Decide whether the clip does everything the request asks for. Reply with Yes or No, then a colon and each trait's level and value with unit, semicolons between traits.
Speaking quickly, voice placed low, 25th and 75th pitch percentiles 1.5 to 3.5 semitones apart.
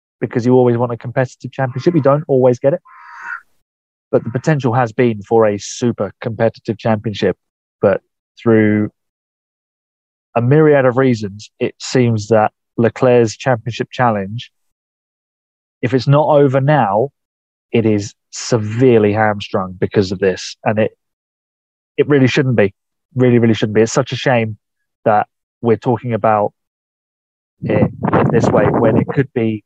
No: average, 145 wpm; low, 120 Hz; average, 3.0 semitones